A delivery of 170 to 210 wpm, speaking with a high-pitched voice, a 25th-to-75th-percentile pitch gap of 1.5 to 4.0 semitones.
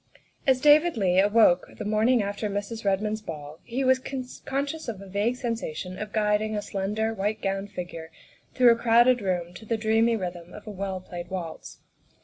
Yes: average, 185 wpm; high, 210 Hz; average, 3.4 semitones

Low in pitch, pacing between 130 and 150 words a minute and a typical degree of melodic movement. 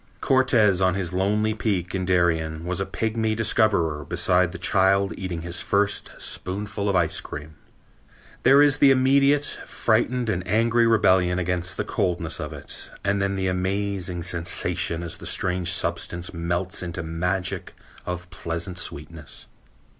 Yes: very low, 95 Hz; average, 145 wpm; average, 3.4 semitones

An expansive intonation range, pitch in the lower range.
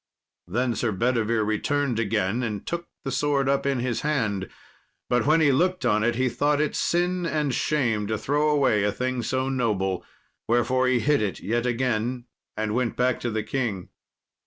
No: average, 4.2 semitones; low, 125 Hz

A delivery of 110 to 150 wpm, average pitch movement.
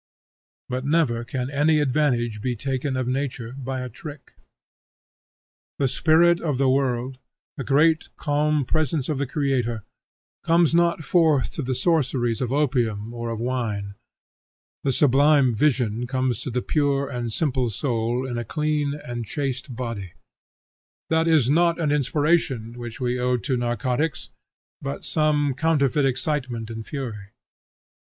Yes: average, 145 wpm; average, 3.6 semitones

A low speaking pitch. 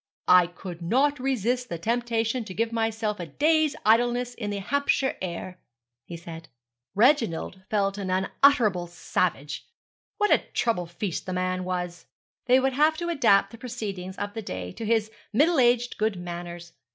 No: high, 210 Hz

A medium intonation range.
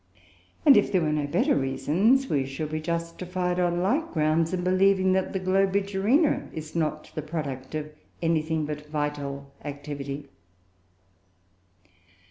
Yes: average, 4.0 semitones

